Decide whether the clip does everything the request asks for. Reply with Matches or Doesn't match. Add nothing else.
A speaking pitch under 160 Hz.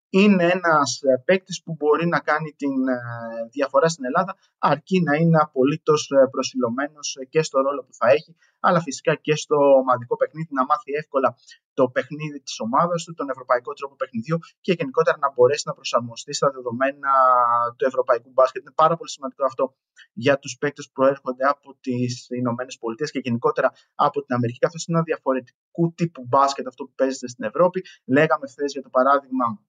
Matches